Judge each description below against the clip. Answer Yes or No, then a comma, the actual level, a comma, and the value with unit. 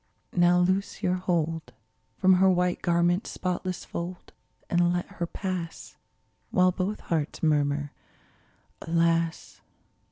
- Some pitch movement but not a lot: No, narrow, 1.8 semitones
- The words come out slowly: Yes, slow, 120 wpm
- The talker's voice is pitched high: No, medium, 175 Hz